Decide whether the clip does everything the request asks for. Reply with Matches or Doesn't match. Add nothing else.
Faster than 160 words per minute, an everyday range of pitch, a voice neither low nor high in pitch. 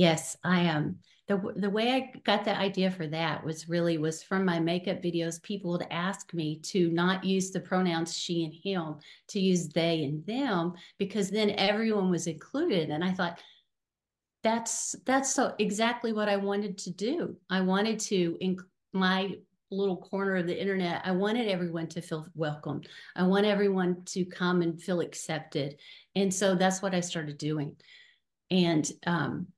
Matches